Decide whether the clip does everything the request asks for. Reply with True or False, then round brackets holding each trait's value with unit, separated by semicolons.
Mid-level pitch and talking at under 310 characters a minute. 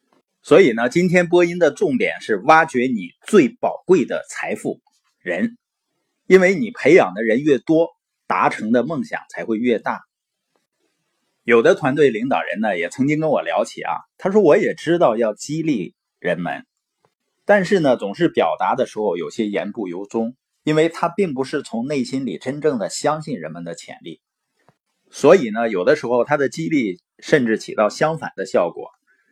True (160 Hz; 250 characters per minute)